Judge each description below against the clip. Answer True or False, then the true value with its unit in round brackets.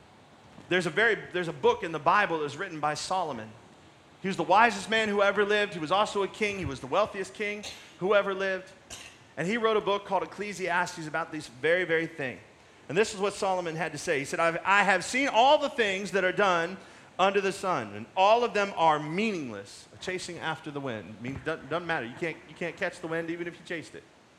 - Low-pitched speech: False (180 Hz)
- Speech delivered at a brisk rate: True (235 wpm)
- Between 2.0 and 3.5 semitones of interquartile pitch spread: False (4.0 semitones)